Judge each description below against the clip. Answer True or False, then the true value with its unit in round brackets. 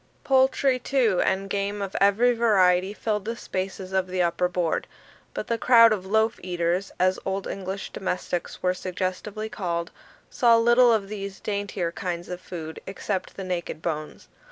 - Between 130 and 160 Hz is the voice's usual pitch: False (195 Hz)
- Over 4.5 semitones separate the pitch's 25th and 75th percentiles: False (3.2 semitones)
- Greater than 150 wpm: True (160 wpm)